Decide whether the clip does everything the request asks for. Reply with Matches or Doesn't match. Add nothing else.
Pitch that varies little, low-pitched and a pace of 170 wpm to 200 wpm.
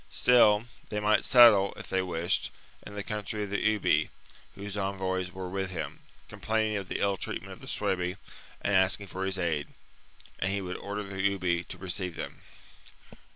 Matches